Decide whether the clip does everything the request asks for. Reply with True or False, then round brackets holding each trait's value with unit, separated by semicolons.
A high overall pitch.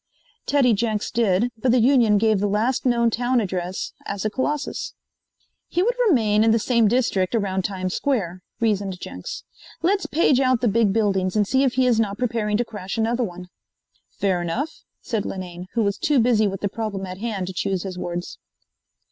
True (215 Hz)